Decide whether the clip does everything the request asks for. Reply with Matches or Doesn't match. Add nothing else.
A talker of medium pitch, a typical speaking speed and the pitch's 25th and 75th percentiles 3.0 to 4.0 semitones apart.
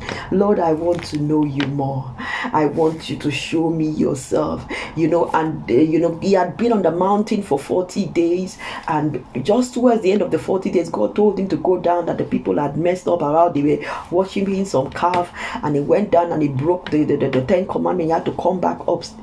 Doesn't match